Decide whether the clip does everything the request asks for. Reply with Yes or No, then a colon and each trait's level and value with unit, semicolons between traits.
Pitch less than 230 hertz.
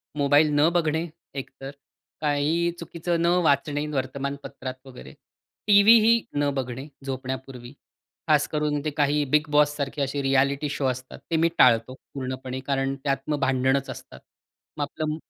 Yes: medium, 140 Hz